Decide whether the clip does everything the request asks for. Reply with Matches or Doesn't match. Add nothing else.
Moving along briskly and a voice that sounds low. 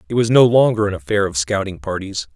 Matches